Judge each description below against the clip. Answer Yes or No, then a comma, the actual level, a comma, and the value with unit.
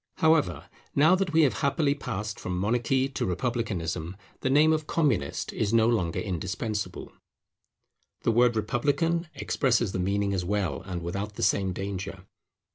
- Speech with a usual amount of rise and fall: No, wide, 6.5 semitones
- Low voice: Yes, low, 110 Hz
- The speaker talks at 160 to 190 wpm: No, average, 150 wpm